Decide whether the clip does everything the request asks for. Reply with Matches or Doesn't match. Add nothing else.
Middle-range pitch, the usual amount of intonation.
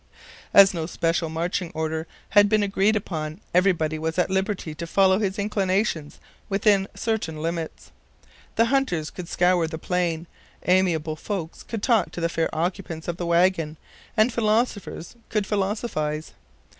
Matches